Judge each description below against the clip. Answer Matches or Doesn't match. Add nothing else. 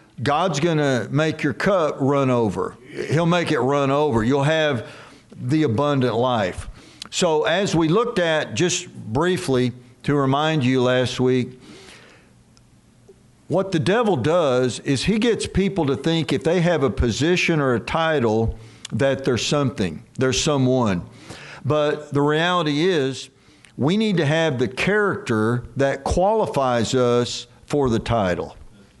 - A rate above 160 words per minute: Doesn't match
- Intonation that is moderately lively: Matches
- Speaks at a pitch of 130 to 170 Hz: Matches